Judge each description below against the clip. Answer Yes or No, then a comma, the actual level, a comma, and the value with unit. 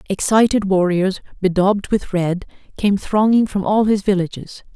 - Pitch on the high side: Yes, high, 195 Hz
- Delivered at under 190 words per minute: Yes, average, 140 wpm